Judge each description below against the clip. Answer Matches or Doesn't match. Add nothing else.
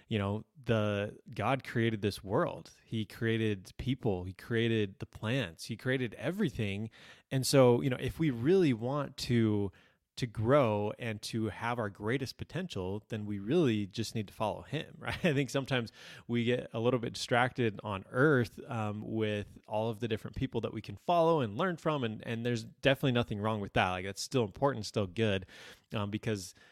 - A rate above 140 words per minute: Matches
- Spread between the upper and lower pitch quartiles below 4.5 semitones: Matches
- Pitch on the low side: Matches